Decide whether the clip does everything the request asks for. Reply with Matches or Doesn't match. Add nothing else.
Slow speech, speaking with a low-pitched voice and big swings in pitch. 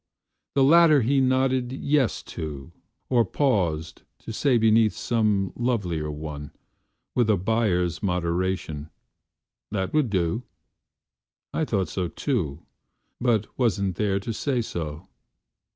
Matches